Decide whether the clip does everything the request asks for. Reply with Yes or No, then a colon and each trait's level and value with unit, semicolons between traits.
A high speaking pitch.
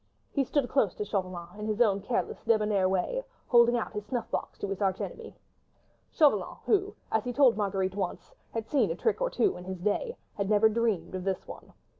Yes: high, 210 Hz